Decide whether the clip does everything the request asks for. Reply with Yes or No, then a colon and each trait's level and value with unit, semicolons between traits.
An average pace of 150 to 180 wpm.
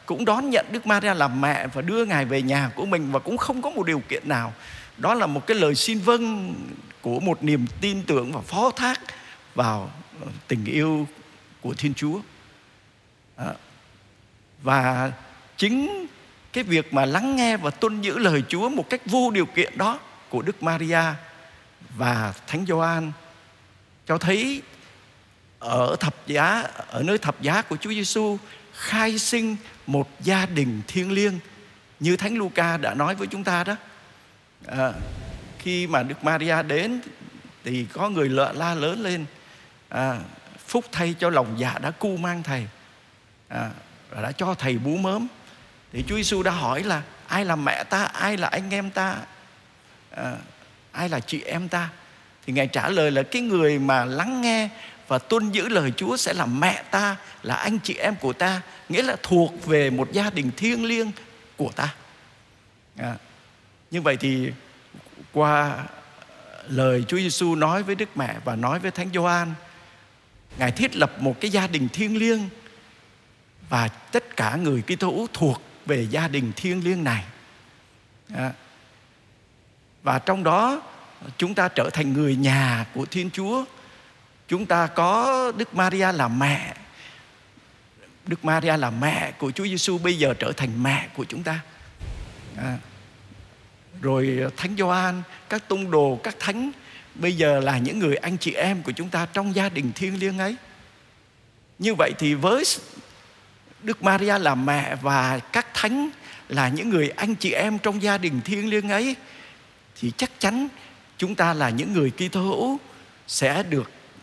Yes: slow, 165 wpm